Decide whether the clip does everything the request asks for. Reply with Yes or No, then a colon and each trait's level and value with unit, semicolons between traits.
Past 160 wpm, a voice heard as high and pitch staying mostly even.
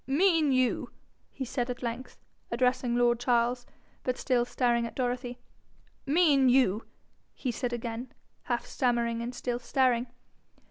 No: average, 145 wpm; high, 245 Hz; narrow, 1.4 semitones